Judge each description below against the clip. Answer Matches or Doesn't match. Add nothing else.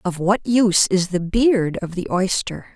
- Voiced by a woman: Matches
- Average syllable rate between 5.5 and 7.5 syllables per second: Doesn't match